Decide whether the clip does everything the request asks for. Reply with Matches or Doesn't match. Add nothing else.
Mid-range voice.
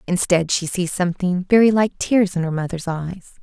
Matches